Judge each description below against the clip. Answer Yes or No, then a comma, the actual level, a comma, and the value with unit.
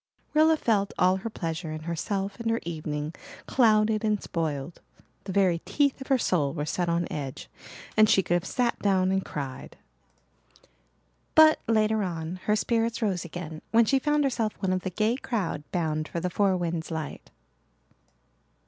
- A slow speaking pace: No, average, 170 wpm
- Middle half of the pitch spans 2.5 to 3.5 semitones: No, average, 5.0 semitones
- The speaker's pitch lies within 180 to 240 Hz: Yes, high, 190 Hz